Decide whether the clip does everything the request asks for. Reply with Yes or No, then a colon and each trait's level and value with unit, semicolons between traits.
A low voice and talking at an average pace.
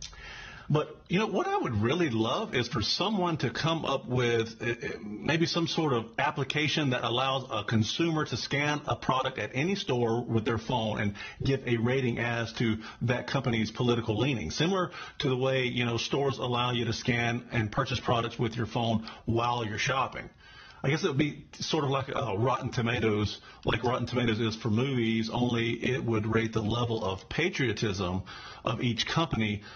Yes: low, 120 Hz; average, 190 wpm